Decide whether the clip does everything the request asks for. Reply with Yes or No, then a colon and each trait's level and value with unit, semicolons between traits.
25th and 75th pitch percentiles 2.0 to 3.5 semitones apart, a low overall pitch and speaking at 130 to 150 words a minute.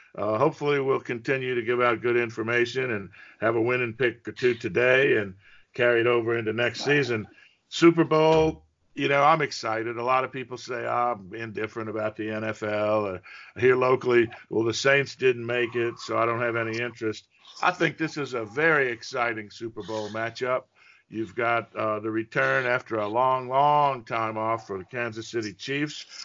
No: narrow, 2.6 semitones; low, 120 Hz; average, 185 wpm